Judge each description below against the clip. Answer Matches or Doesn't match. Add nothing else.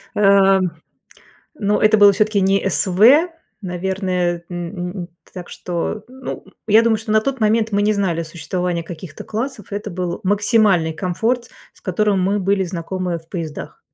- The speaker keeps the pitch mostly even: Doesn't match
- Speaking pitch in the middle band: Doesn't match